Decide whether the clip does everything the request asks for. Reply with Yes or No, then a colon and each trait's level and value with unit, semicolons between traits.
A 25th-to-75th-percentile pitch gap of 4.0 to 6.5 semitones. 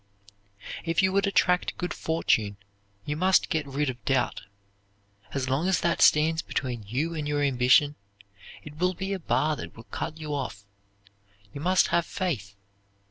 Yes: average, 4.6 semitones